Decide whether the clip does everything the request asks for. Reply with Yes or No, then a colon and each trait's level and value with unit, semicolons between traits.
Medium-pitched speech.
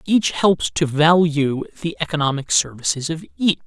Yes: medium, 155 Hz